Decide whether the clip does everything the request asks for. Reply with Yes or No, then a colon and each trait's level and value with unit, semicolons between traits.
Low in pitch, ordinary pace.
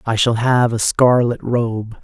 Yes: low, 115 Hz; average, 175 wpm